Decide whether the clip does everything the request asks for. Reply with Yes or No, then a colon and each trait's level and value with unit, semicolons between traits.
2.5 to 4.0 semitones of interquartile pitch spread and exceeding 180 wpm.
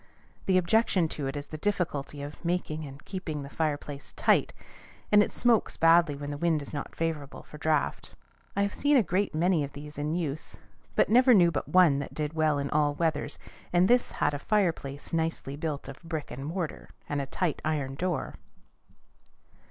Yes: average, 3.7 semitones; average, 190 wpm